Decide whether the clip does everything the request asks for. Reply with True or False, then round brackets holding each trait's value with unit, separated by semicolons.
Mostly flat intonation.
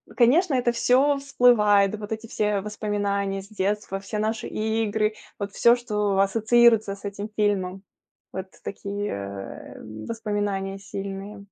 True (2.1 semitones)